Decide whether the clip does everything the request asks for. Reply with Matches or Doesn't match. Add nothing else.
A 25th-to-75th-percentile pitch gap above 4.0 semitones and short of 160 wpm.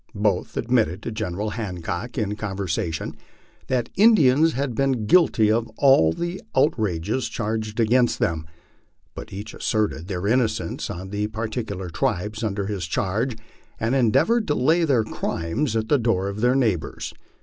Matches